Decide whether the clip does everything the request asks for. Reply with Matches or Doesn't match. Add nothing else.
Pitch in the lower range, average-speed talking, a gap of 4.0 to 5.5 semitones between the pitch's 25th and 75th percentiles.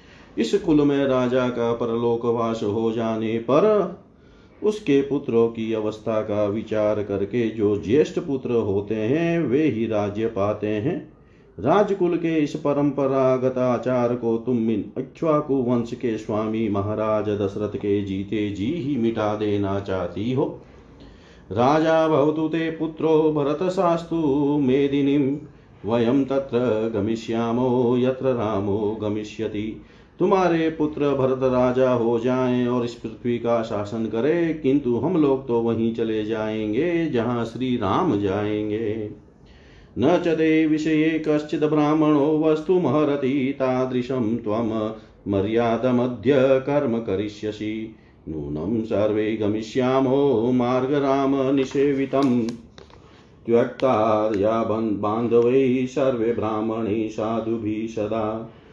Doesn't match